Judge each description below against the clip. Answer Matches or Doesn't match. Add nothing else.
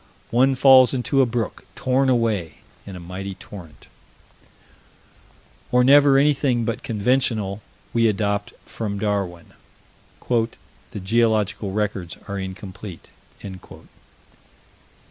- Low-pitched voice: Matches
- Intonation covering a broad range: Doesn't match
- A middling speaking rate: Doesn't match